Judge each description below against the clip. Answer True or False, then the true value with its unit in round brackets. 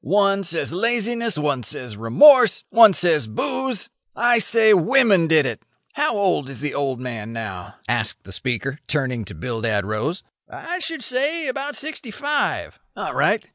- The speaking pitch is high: False (180 Hz)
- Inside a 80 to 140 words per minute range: False (160 wpm)